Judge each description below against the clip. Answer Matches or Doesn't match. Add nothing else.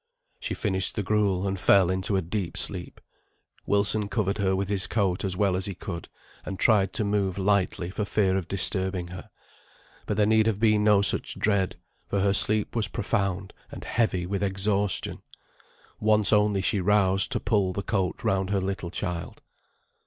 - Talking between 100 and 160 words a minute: Doesn't match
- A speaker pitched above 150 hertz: Doesn't match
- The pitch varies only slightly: Matches